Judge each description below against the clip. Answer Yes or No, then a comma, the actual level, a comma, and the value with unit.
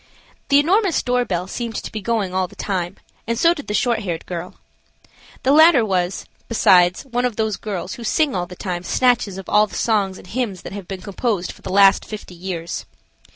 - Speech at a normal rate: No, fast, 210 wpm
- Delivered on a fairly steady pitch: No, average, 4.9 semitones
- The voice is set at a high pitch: Yes, high, 205 Hz